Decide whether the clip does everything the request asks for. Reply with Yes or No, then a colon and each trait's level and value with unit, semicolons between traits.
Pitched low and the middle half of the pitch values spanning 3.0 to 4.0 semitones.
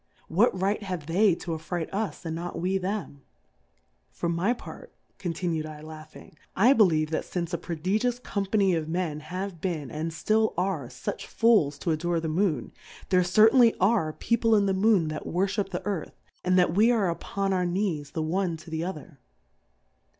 No: medium, 180 Hz; average, 3.7 semitones